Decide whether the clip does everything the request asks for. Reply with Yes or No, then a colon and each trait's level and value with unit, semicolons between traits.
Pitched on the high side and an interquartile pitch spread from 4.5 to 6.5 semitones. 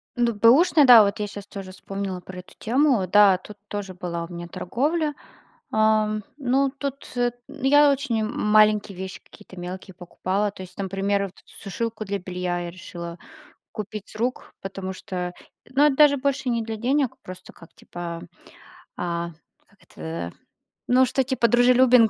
Yes: high, 210 Hz; average, 5.1 semitones